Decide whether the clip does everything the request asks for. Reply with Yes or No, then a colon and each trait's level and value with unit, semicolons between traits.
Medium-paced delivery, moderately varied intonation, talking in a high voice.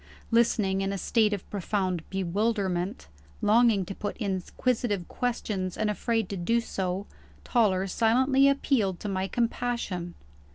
No: slow, 130 wpm; average, 3.6 semitones; high, 205 Hz